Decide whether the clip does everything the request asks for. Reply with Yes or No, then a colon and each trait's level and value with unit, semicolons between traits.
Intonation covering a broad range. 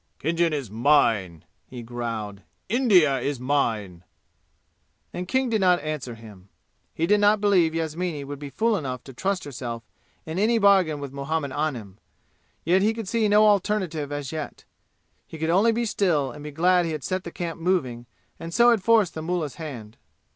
Yes: wide, 6.3 semitones